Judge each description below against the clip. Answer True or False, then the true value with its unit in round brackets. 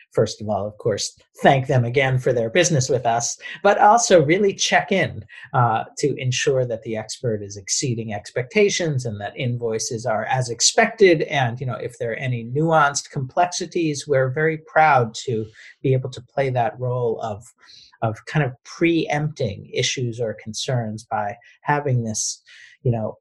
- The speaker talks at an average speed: True (170 wpm)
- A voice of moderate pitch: False (130 Hz)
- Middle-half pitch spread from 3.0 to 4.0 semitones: False (5.2 semitones)